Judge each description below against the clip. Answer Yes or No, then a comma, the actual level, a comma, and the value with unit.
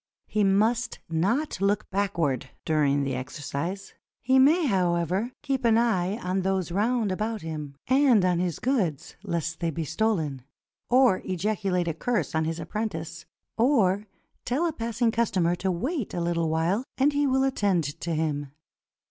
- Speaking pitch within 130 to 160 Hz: No, high, 190 Hz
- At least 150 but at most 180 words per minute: Yes, average, 155 wpm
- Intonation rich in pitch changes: Yes, wide, 5.9 semitones